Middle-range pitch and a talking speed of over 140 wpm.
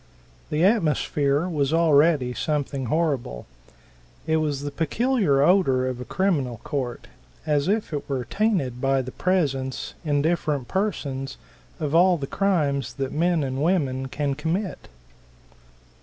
No: medium, 145 Hz; slow, 135 wpm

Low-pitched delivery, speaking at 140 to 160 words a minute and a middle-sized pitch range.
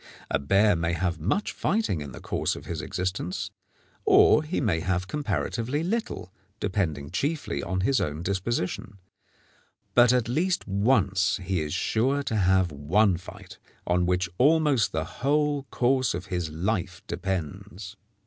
No: very low, 95 Hz; average, 150 wpm; wide, 6.2 semitones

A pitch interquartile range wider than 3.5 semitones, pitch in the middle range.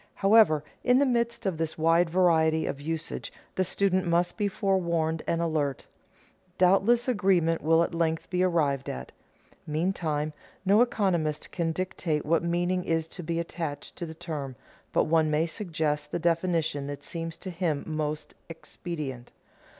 No: average, 2.8 semitones; medium, 165 Hz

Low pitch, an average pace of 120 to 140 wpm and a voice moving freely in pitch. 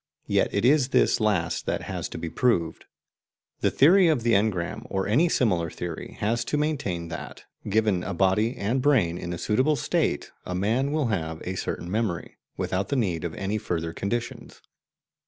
No: low, 105 Hz; average, 180 wpm; wide, 6.1 semitones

